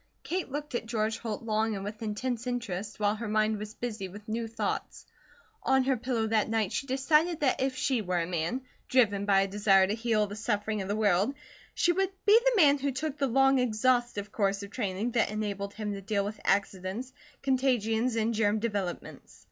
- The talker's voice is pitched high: Yes, high, 220 Hz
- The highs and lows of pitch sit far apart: No, average, 3.8 semitones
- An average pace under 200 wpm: No, fast, 205 wpm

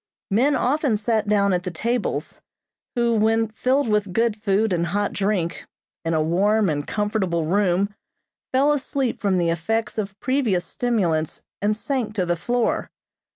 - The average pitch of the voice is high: Yes, high, 210 Hz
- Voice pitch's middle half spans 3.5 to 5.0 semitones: Yes, average, 4.2 semitones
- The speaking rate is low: No, average, 155 wpm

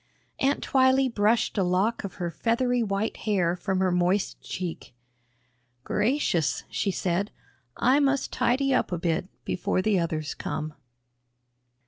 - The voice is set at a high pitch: Yes, high, 200 Hz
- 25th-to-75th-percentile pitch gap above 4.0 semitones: Yes, wide, 5.5 semitones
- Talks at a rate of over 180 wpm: No, slow, 135 wpm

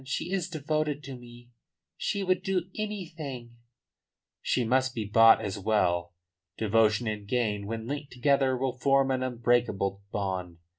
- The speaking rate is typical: Yes, average, 150 wpm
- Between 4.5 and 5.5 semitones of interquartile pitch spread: Yes, average, 4.8 semitones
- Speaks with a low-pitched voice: Yes, low, 125 Hz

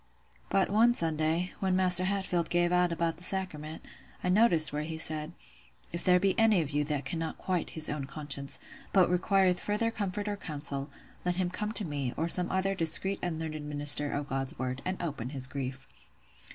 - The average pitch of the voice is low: No, medium, 170 Hz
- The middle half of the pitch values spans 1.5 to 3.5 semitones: No, average, 4.1 semitones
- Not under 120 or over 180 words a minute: No, average, 190 wpm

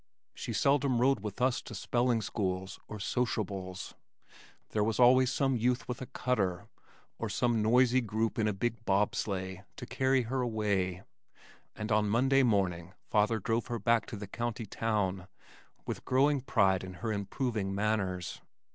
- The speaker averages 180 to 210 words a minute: No, average, 160 wpm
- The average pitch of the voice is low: Yes, low, 110 Hz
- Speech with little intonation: No, average, 3.9 semitones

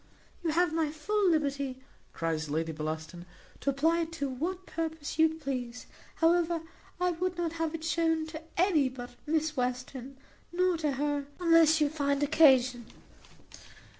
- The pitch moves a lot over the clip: No, average, 3.9 semitones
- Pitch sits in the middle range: No, very high, 310 Hz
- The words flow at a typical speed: Yes, average, 150 wpm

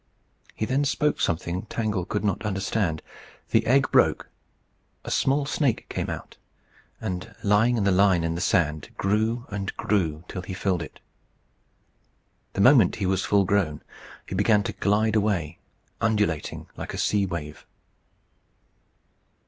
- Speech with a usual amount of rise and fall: Yes, average, 3.4 semitones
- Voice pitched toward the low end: Yes, low, 100 Hz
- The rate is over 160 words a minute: No, average, 150 wpm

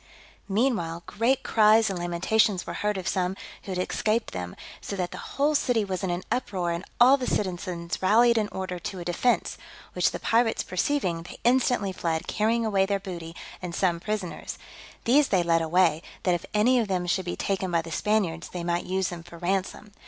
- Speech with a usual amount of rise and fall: Yes, average, 3.9 semitones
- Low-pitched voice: No, high, 190 Hz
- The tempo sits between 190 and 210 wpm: Yes, average, 200 wpm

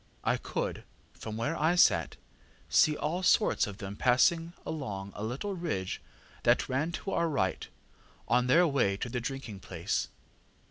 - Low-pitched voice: Yes, low, 130 Hz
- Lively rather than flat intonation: Yes, wide, 8.1 semitones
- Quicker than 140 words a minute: Yes, average, 155 wpm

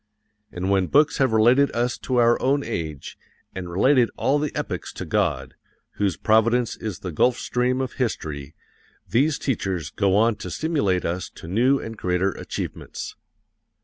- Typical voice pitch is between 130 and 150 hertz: No, low, 115 Hz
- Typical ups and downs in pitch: No, wide, 5.7 semitones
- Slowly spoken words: No, average, 160 wpm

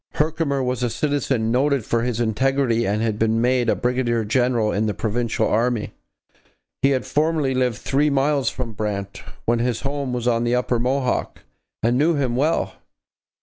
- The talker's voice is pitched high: No, low, 125 Hz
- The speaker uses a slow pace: No, average, 175 wpm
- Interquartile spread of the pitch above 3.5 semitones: No, average, 3.0 semitones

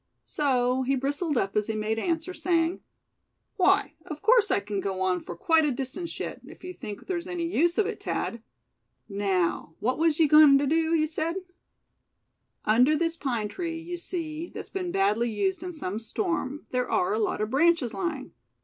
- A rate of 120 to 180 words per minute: No, average, 190 wpm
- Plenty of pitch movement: Yes, wide, 7.2 semitones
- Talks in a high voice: Yes, very high, 290 Hz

